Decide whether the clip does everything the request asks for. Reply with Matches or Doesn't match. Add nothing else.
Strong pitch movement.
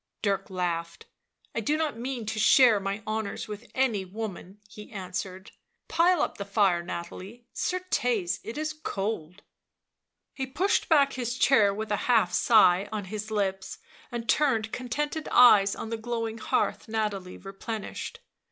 Doesn't match